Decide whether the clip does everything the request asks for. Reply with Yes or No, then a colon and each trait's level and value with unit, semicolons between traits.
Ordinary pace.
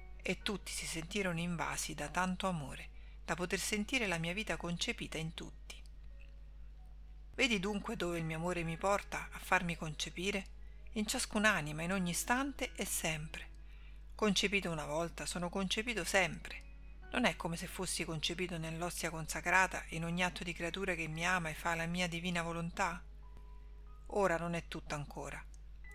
Yes: average, 155 wpm